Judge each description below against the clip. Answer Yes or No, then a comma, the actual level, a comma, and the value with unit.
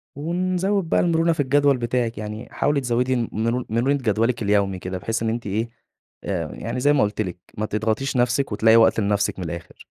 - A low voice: Yes, low, 115 Hz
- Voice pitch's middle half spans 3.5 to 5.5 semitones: Yes, average, 4.6 semitones